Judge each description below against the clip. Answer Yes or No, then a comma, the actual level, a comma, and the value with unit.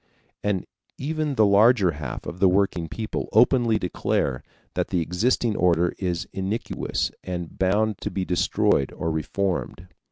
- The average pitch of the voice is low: Yes, very low, 95 Hz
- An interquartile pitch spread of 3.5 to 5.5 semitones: Yes, average, 3.8 semitones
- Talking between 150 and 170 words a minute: No, average, 140 wpm